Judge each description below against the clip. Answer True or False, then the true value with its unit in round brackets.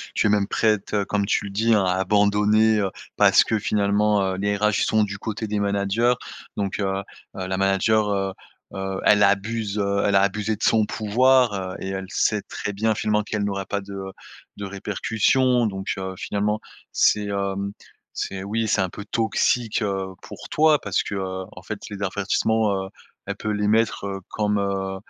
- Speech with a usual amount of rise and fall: False (1.6 semitones)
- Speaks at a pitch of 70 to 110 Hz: True (100 Hz)